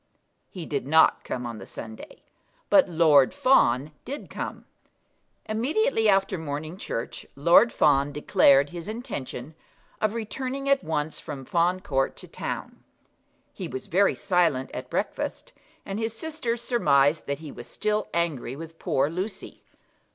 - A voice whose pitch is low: No, medium, 165 Hz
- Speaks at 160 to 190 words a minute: No, average, 145 wpm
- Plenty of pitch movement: Yes, wide, 7.4 semitones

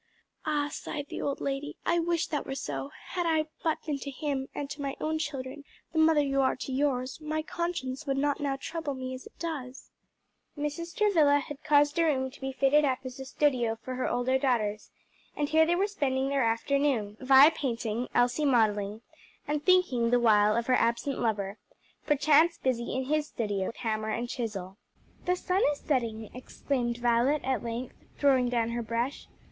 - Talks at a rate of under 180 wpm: No, average, 190 wpm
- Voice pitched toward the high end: Yes, very high, 270 Hz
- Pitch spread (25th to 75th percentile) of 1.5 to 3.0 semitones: No, average, 3.7 semitones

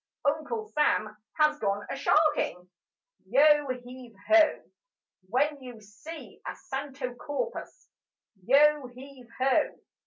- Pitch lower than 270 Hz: No, very high, 275 Hz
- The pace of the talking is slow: Yes, slow, 105 wpm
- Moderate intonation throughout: Yes, average, 3.5 semitones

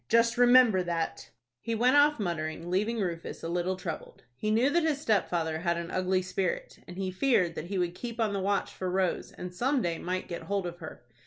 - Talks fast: Yes, fast, 220 wpm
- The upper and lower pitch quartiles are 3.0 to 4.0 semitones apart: No, average, 4.9 semitones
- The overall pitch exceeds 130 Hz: Yes, medium, 185 Hz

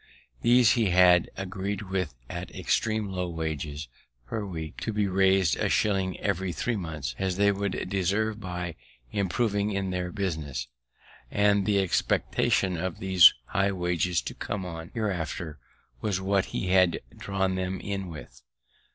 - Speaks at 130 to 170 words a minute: Yes, average, 150 wpm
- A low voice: Yes, very low, 95 Hz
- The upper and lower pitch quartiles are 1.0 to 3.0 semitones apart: Yes, narrow, 2.4 semitones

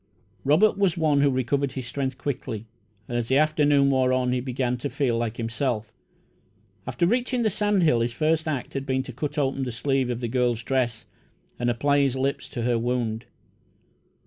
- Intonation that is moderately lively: Yes, average, 3.0 semitones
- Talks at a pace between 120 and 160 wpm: No, average, 195 wpm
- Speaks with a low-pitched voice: Yes, low, 130 Hz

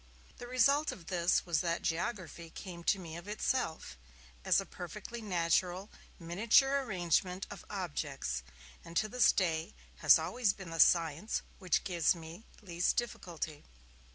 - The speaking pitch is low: No, medium, 180 Hz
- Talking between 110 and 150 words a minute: Yes, average, 145 wpm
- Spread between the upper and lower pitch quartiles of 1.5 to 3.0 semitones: No, average, 4.1 semitones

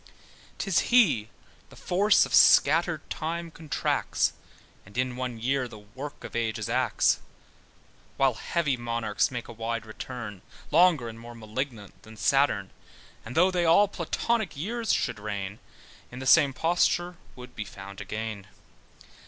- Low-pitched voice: Yes, low, 125 Hz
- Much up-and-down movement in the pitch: Yes, wide, 7.0 semitones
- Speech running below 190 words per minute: Yes, average, 145 wpm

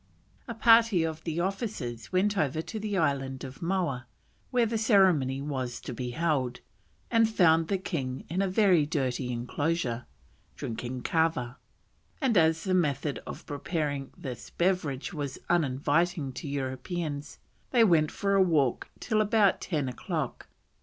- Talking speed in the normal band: Yes, average, 145 wpm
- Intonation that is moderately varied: No, wide, 6.1 semitones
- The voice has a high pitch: No, medium, 160 Hz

